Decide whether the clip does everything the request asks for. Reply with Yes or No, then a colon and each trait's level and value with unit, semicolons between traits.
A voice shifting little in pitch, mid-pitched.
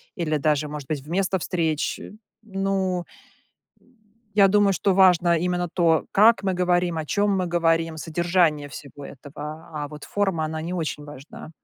No: average, 3.3 semitones; medium, 170 Hz